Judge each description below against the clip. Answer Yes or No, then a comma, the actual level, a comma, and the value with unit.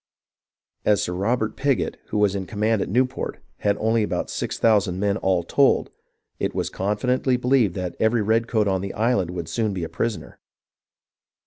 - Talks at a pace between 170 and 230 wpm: Yes, average, 175 wpm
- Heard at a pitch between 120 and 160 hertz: No, low, 105 Hz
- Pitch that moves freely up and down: No, average, 3.1 semitones